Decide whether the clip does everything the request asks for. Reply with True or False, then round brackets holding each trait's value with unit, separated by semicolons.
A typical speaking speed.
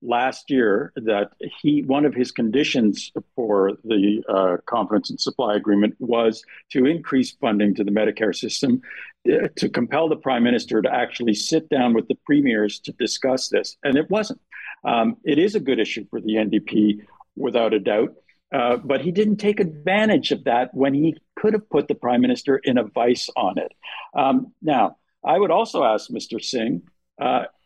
True (180 wpm)